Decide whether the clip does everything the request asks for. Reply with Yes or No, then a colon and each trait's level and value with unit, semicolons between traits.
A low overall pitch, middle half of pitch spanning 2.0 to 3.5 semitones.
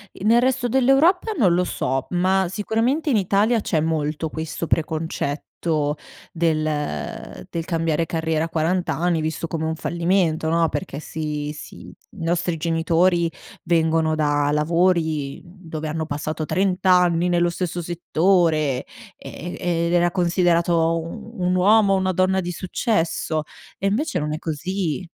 No: medium, 170 Hz; average, 2.7 semitones